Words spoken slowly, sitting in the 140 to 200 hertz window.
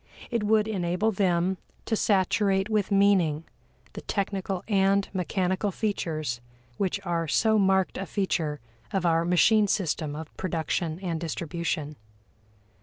Yes: slow, 125 wpm; high, 190 Hz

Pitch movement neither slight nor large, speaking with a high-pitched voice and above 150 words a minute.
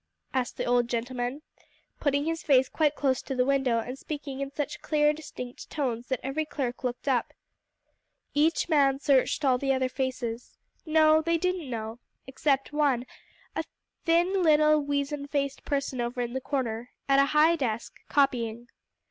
Yes: average, 3.1 semitones; very high, 275 Hz; average, 165 wpm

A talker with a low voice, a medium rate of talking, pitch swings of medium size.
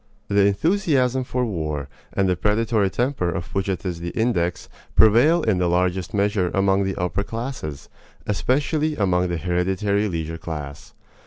Yes: very low, 95 Hz; average, 155 wpm; average, 4.6 semitones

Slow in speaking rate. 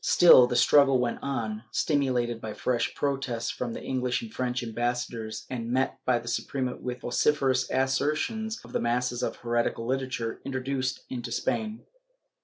No: average, 155 wpm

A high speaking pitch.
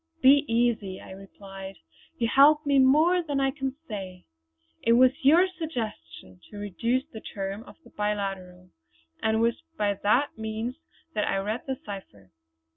Yes: high, 220 Hz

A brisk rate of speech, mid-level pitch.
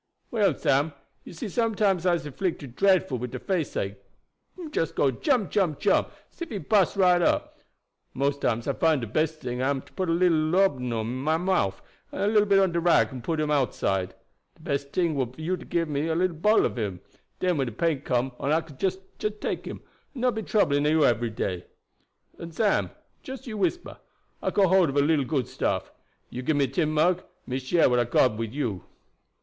Yes: fast, 220 wpm; medium, 155 Hz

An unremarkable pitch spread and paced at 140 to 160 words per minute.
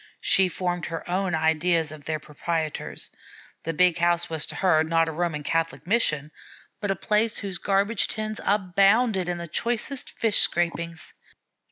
Yes: average, 3.4 semitones; average, 155 wpm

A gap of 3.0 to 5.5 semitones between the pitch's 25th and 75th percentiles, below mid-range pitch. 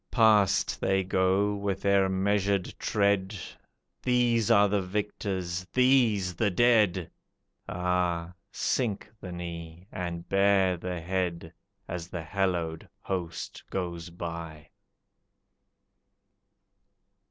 No: narrow, 2.6 semitones; very low, 95 Hz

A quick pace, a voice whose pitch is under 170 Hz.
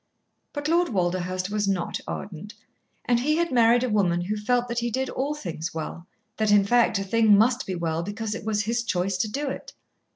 No: fast, 215 wpm; high, 215 Hz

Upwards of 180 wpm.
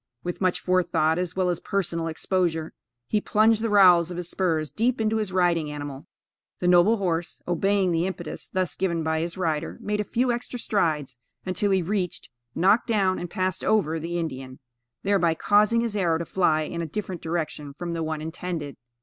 Yes: average, 190 wpm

